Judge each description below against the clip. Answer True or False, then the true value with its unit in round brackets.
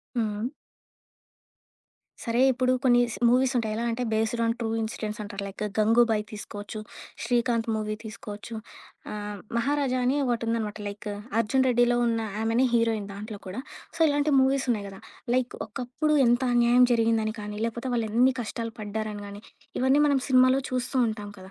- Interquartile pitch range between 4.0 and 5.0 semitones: False (2.6 semitones)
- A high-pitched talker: True (230 Hz)